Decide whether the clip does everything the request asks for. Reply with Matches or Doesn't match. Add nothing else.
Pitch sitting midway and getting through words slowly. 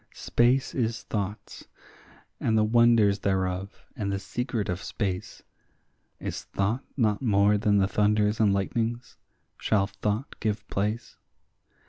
Doesn't match